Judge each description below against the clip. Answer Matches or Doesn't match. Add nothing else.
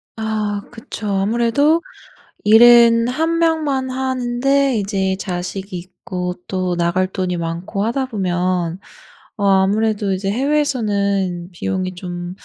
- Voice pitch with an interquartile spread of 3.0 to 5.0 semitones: Matches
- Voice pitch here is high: Matches